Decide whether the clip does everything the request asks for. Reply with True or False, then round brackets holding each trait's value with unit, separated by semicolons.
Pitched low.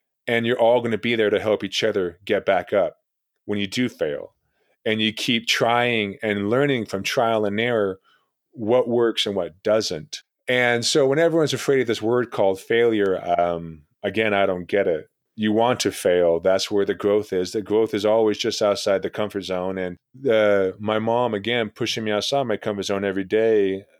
True (110 Hz)